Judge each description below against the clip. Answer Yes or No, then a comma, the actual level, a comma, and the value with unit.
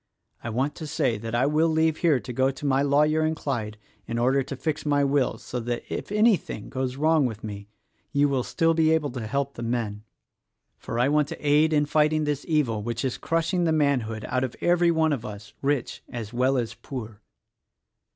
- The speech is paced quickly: Yes, fast, 215 wpm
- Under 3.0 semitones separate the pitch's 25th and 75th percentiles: No, average, 4.3 semitones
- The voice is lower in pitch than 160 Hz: Yes, medium, 140 Hz